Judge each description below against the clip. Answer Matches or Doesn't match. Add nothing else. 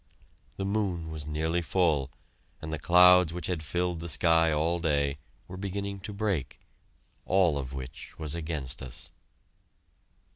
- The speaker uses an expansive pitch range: Doesn't match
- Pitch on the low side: Matches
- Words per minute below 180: Matches